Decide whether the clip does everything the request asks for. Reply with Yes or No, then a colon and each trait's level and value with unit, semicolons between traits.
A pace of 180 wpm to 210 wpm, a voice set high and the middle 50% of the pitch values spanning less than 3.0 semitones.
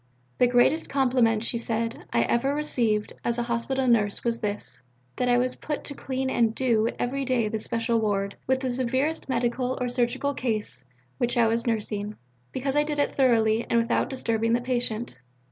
Yes: average, 185 wpm; high, 240 Hz; narrow, 2.4 semitones